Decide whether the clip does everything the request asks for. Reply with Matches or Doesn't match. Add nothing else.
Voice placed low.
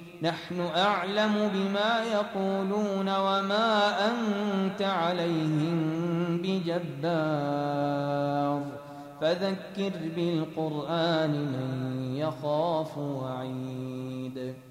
Doesn't match